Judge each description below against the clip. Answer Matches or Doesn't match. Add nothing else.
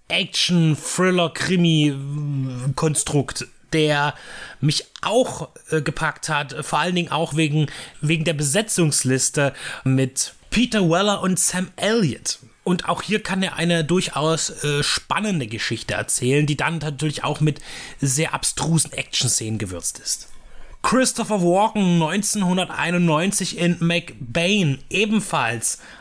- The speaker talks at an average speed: Doesn't match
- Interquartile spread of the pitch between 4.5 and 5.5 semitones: Doesn't match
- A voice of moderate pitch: Matches